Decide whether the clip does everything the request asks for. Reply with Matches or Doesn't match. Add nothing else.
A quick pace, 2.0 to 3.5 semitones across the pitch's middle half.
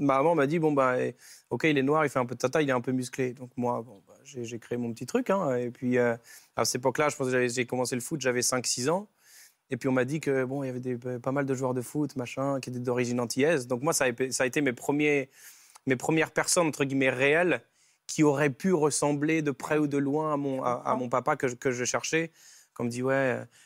Matches